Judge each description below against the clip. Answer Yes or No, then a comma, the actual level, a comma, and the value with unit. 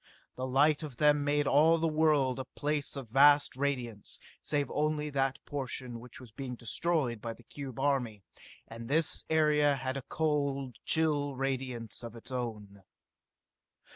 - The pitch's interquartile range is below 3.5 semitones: Yes, average, 3.0 semitones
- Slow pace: No, average, 155 wpm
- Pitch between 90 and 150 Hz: Yes, low, 135 Hz